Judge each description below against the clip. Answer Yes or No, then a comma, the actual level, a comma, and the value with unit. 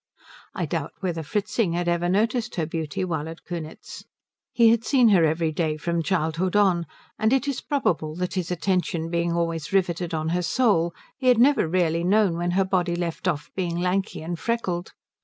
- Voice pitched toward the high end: No, medium, 175 Hz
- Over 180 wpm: Yes, average, 190 wpm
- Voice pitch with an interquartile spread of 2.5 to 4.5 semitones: Yes, average, 2.9 semitones